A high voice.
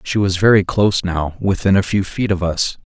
No: very low, 95 Hz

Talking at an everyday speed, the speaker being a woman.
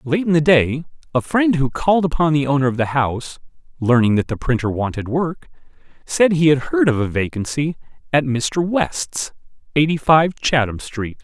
No: average, 180 wpm; male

